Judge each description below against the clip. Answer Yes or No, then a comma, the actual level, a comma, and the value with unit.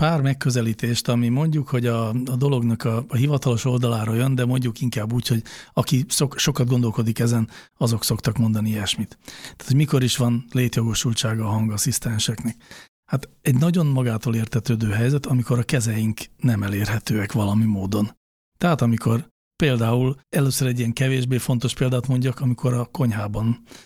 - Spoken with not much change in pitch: Yes, narrow, 2.3 semitones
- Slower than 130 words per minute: No, fast, 155 wpm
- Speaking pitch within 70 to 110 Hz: No, low, 120 Hz